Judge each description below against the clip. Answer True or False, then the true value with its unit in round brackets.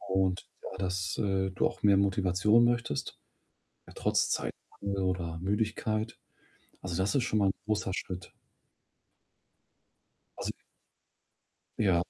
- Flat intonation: True (2.3 semitones)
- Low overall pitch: True (95 Hz)